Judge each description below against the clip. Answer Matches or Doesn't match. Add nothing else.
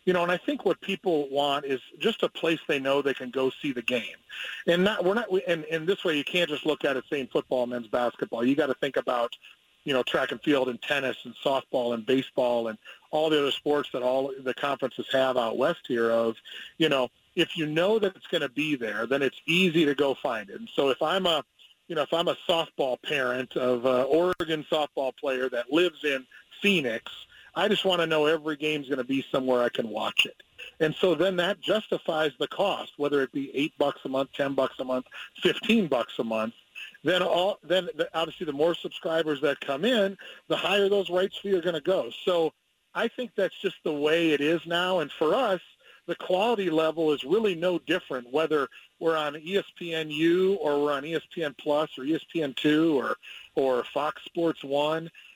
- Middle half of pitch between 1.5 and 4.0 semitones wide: Doesn't match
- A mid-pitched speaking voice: Matches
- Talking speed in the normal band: Doesn't match